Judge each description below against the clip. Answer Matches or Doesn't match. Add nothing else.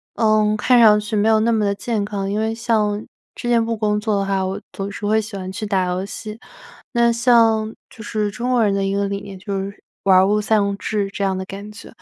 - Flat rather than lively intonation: Matches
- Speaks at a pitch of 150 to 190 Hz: Doesn't match